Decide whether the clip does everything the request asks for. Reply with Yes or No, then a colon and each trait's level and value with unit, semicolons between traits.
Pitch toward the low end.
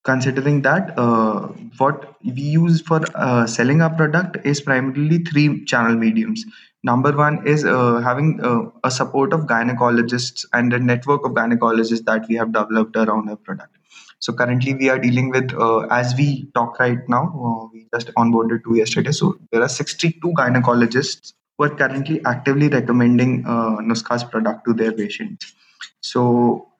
Yes: low, 125 Hz